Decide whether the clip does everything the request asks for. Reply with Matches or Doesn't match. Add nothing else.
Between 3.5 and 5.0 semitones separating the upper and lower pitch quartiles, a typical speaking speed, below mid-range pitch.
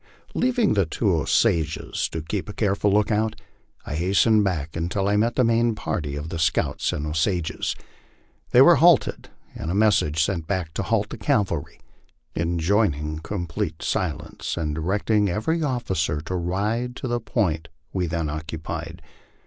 Matches